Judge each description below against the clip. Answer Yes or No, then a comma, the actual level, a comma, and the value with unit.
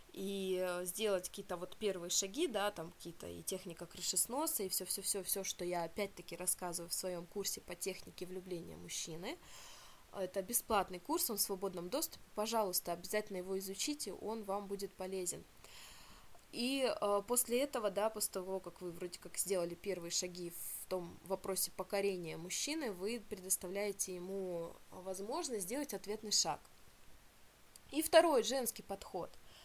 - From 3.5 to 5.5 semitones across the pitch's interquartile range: No, average, 2.7 semitones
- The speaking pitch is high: Yes, high, 195 Hz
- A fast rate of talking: No, average, 140 wpm